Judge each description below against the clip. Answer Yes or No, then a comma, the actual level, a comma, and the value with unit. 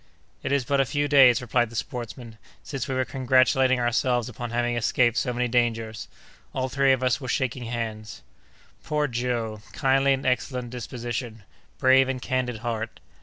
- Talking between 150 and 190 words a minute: Yes, average, 170 wpm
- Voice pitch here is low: Yes, low, 125 Hz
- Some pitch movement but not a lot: No, narrow, 1.9 semitones